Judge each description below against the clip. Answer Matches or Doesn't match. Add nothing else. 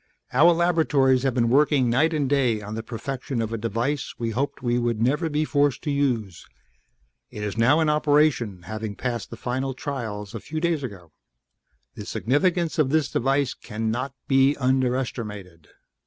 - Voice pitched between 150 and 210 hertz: Doesn't match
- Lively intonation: Doesn't match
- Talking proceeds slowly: Doesn't match